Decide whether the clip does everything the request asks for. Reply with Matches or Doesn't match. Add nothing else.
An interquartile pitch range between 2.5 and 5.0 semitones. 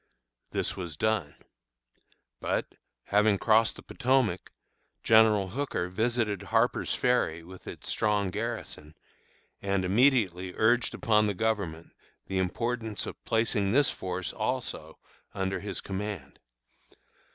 Matches